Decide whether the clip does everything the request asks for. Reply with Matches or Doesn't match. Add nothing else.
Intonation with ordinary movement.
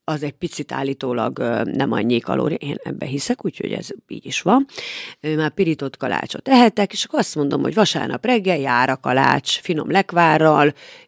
Doesn't match